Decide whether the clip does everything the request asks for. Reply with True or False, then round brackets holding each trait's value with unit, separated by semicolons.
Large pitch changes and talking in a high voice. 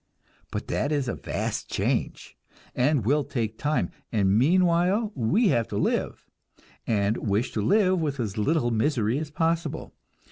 False (6.8 semitones; 140 Hz)